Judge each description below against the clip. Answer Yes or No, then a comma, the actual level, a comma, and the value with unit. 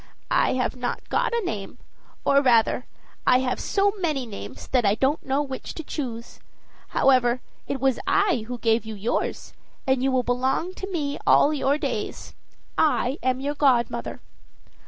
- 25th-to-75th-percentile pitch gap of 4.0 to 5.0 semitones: No, average, 3.1 semitones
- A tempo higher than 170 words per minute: No, average, 165 wpm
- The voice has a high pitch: Yes, very high, 260 Hz